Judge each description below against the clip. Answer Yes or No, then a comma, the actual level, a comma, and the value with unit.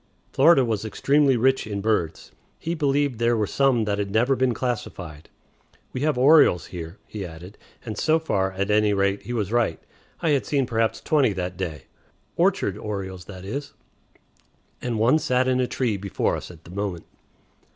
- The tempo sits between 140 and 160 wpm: No, average, 180 wpm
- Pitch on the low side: Yes, low, 110 Hz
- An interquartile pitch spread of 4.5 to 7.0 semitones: Yes, average, 5.2 semitones